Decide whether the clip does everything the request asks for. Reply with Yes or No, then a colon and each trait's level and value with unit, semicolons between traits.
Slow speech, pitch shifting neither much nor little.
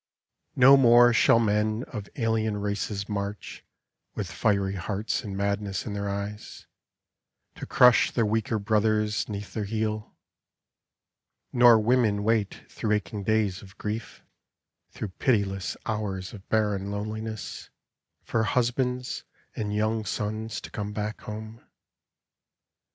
No: slow, 125 wpm; narrow, 1.7 semitones